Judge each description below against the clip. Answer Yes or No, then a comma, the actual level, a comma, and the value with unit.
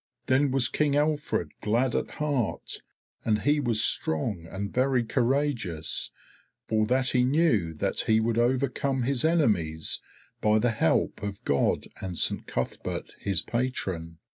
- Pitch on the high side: No, low, 120 Hz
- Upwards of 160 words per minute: No, average, 140 wpm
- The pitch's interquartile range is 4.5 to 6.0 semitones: Yes, average, 5.3 semitones